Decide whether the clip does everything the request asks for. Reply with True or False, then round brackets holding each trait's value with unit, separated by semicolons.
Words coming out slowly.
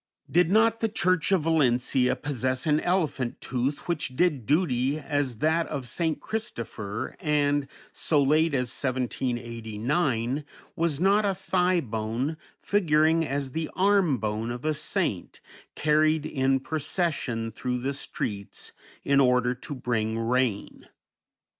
True (130 wpm)